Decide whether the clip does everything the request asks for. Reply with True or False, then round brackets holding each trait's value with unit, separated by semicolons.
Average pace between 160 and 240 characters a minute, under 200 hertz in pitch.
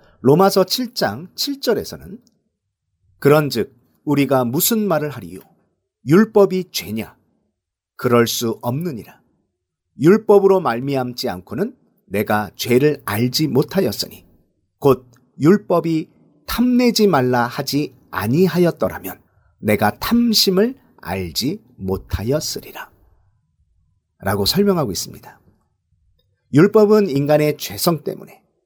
True (225 characters per minute; 135 Hz)